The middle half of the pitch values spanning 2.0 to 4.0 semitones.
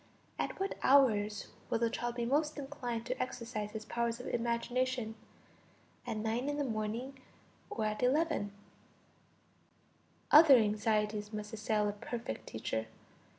Yes: average, 3.2 semitones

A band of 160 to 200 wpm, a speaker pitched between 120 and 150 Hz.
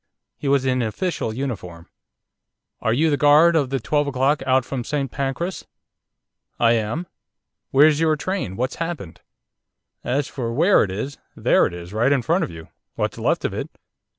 Yes: average, 170 wpm; low, 135 Hz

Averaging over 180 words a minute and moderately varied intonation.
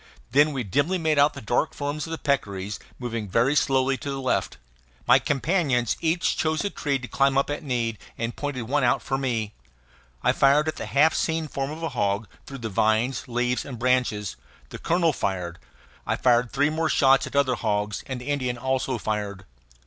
Yes: average, 195 wpm; average, 3.8 semitones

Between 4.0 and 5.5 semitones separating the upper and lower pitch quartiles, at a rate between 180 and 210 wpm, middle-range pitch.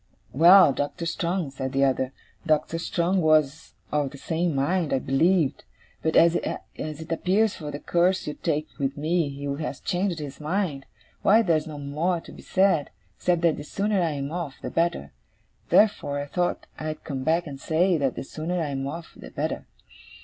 No: average, 3.5 semitones; average, 185 wpm; medium, 160 Hz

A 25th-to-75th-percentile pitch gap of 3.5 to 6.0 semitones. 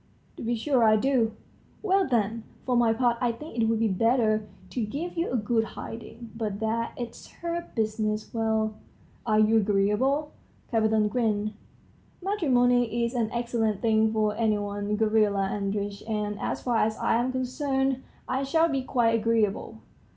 No: narrow, 2.5 semitones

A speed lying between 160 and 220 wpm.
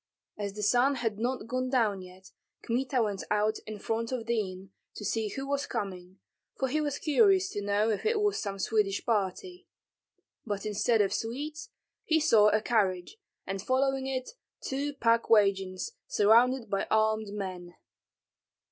Yes: average, 165 wpm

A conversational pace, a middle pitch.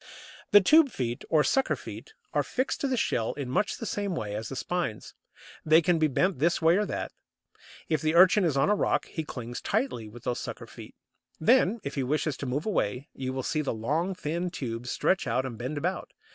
No: fast, 220 wpm; medium, 155 Hz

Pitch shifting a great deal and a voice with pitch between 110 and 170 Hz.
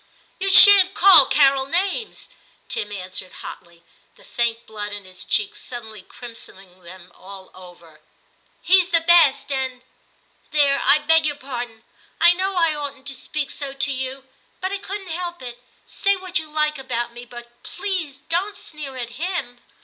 No: wide, 6.6 semitones; very high, 275 Hz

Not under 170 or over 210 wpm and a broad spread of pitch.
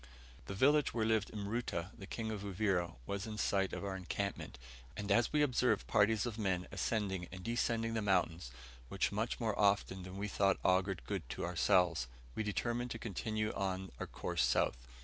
No: average, 180 wpm; average, 2.9 semitones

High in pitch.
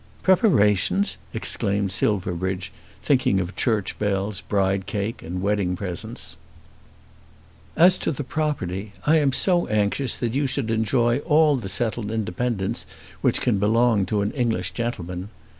No: low, 105 Hz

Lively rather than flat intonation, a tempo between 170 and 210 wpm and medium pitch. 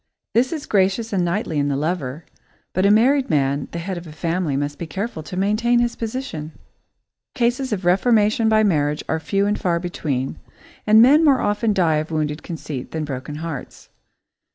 Yes: wide, 6.1 semitones; average, 185 wpm; medium, 180 Hz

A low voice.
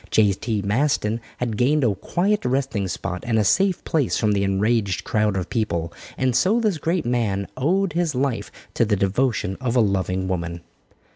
Yes: low, 115 Hz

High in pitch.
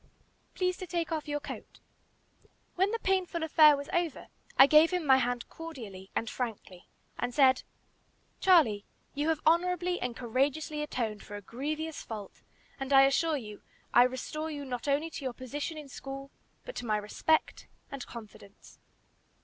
Yes: very high, 280 Hz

